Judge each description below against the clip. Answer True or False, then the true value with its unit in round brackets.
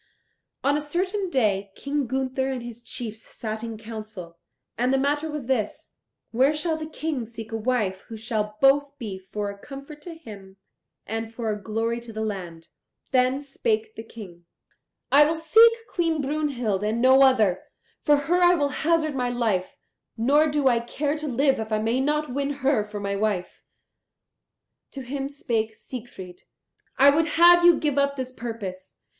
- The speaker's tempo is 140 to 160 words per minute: False (175 wpm)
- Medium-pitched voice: False (255 Hz)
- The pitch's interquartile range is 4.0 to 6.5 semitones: True (5.1 semitones)